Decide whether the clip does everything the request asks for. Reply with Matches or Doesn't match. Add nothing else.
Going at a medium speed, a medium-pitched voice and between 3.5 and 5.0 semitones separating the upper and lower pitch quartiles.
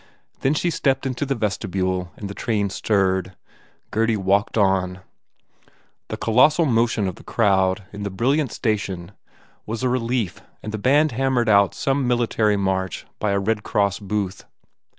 Doesn't match